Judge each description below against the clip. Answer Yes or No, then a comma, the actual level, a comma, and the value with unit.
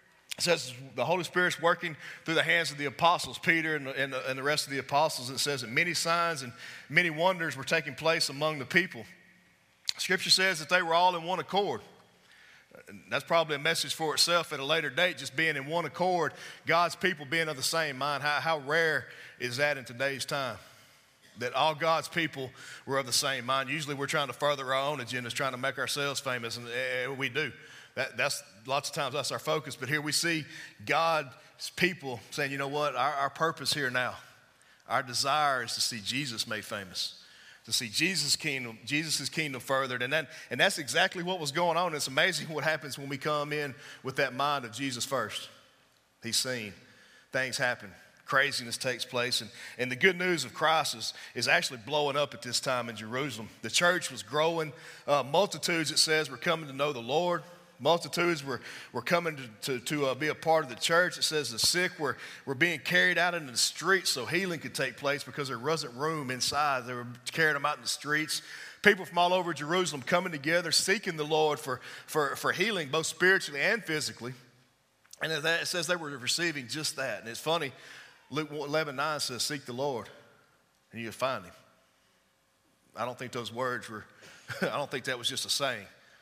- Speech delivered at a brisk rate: Yes, fast, 210 wpm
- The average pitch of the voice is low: No, medium, 150 Hz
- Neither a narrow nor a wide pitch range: Yes, average, 3.9 semitones